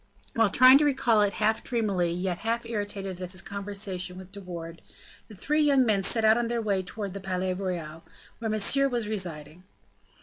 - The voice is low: No, high, 200 Hz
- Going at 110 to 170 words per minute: No, average, 195 wpm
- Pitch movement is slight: No, average, 3.8 semitones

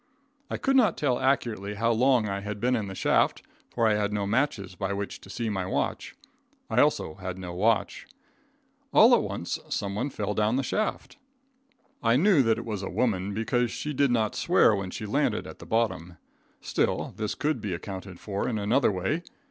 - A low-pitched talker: Yes, low, 105 Hz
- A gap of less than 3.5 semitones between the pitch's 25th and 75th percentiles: No, average, 3.8 semitones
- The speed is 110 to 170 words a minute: No, average, 195 wpm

